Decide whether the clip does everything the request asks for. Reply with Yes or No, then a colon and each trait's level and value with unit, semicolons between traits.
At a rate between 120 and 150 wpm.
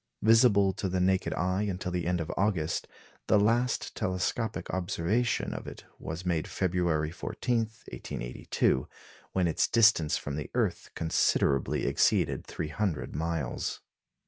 Yes: slow, 135 wpm